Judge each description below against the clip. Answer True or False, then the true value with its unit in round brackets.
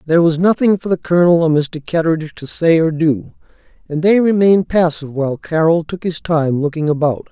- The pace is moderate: True (195 wpm)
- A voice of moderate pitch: True (165 Hz)